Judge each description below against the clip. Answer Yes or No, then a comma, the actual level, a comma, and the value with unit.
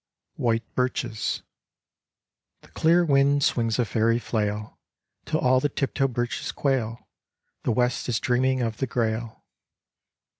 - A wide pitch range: No, narrow, 2.5 semitones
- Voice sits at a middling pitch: No, low, 120 Hz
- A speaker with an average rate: No, slow, 125 wpm